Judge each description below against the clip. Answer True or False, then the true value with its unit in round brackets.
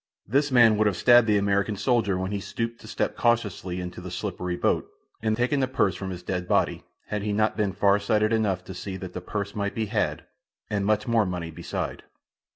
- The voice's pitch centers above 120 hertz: False (100 Hz)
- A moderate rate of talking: False (220 wpm)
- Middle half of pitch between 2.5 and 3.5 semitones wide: True (2.8 semitones)